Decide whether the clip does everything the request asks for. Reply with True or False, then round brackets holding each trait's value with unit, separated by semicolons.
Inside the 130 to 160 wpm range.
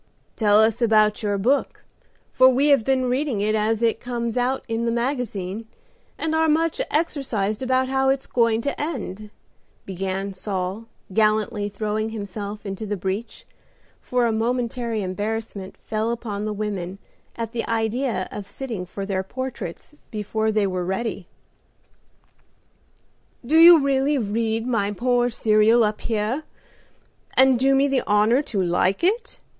True (150 wpm)